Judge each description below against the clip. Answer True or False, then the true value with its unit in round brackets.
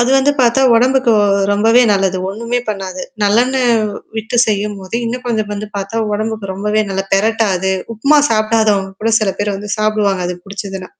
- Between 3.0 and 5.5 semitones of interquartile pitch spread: False (2.6 semitones)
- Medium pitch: False (215 Hz)